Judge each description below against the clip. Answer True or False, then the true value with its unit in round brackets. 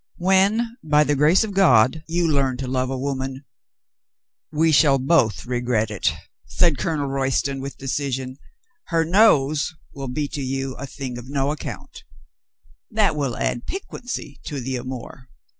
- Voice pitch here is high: False (140 Hz)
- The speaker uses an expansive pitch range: False (3.8 semitones)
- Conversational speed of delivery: True (175 wpm)